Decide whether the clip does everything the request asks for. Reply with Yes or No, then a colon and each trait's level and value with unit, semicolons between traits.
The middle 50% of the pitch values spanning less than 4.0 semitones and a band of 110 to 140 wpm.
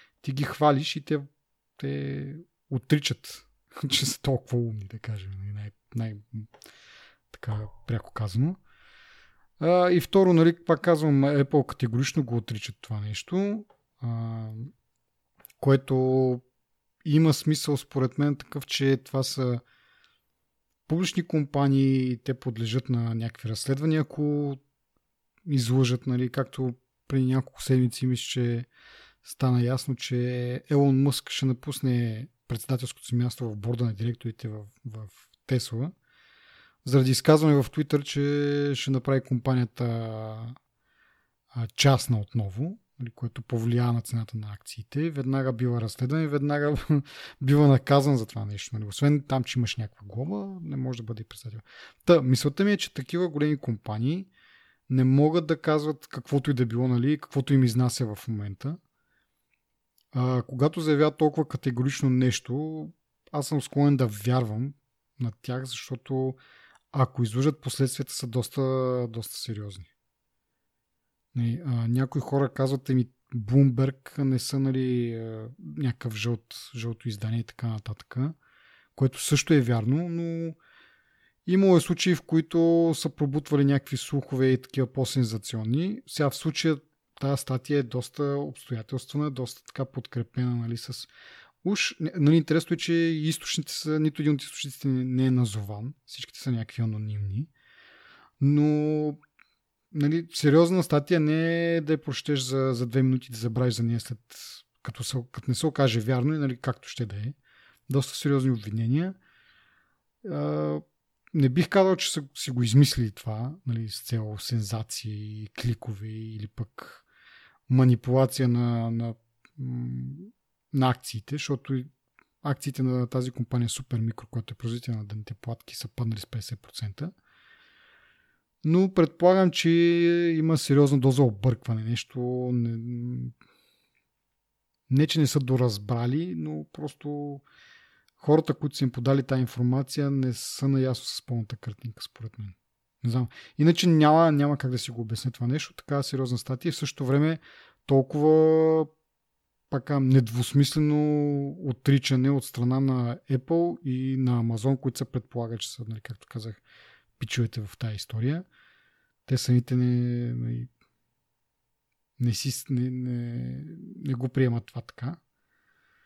Yes: average, 3.6 semitones; average, 135 wpm